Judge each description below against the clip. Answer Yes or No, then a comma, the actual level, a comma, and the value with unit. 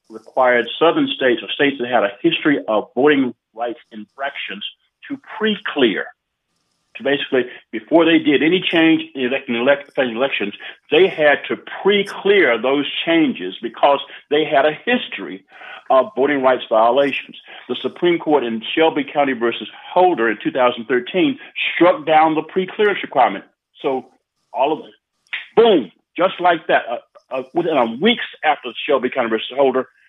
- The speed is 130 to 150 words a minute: Yes, average, 145 wpm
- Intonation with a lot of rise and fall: Yes, wide, 6.9 semitones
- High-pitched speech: No, medium, 155 Hz